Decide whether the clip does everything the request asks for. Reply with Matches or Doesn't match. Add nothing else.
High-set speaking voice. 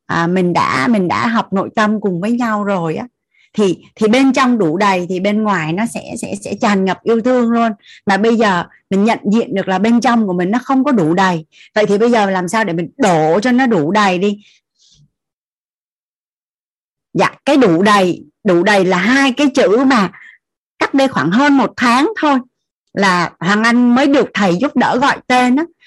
Matches